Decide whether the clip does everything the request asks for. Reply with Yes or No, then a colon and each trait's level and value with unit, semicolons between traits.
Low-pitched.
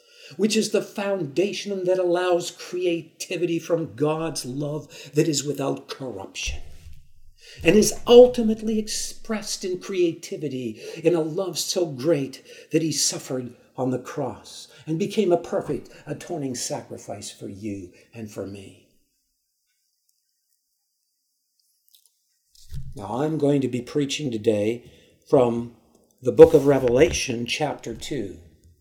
No: medium, 155 Hz